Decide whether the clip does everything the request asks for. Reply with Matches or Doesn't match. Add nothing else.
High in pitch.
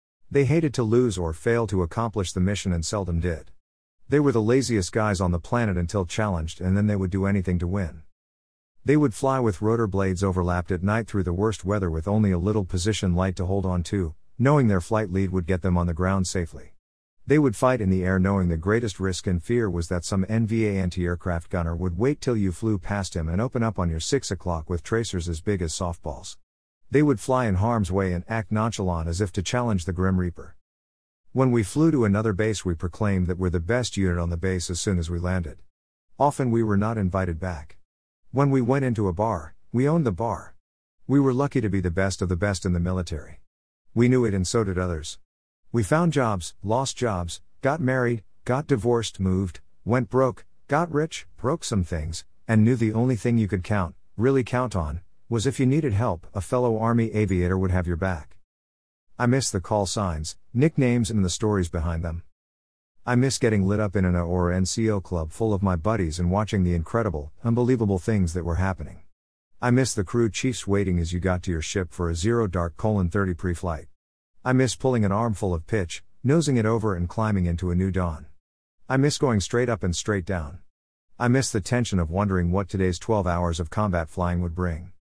Doesn't match